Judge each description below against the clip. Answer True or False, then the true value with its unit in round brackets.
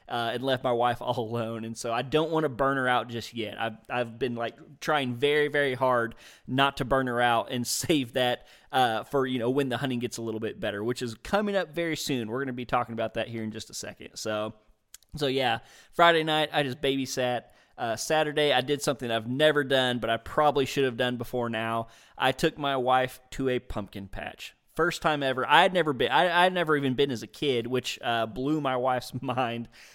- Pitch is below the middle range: True (125 Hz)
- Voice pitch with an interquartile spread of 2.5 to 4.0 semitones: True (3.1 semitones)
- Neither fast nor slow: False (235 wpm)